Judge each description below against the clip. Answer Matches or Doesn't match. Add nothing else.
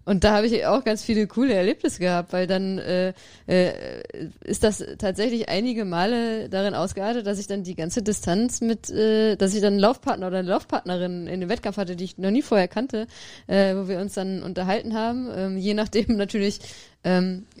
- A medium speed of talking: Doesn't match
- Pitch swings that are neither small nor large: Matches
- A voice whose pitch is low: Doesn't match